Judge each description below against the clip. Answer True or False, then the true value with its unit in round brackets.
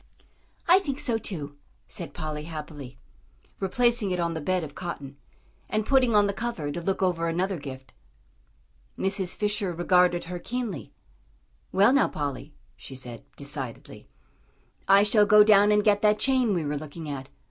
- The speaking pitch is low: False (180 Hz)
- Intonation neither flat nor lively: False (5.7 semitones)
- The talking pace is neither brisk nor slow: True (160 wpm)